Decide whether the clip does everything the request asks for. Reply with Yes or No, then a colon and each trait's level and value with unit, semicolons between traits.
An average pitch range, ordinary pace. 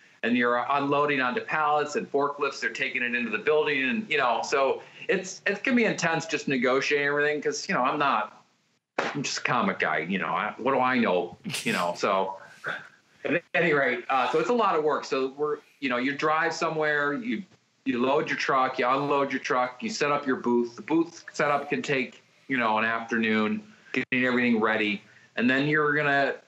No: average, 3.8 semitones; fast, 210 wpm